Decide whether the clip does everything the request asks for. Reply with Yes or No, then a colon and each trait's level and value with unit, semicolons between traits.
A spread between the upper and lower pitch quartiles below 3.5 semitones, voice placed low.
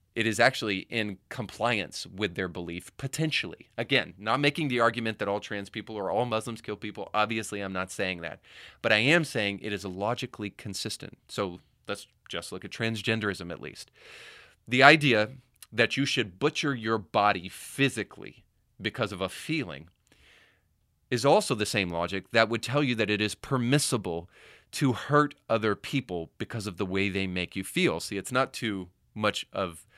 No: average, 4.1 semitones; low, 110 Hz